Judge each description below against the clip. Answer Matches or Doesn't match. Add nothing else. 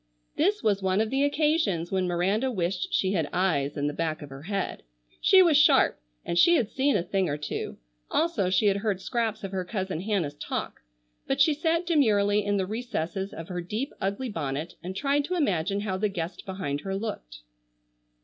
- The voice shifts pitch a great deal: Matches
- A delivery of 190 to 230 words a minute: Matches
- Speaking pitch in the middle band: Doesn't match